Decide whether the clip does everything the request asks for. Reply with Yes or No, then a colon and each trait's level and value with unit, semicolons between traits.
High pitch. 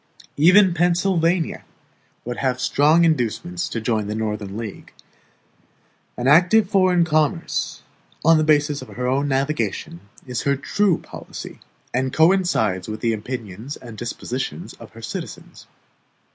No: medium, 140 Hz